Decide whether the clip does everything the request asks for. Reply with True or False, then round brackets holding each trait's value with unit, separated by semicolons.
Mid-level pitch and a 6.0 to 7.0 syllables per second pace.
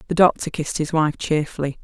True (155 Hz; 6.2 syllables/s)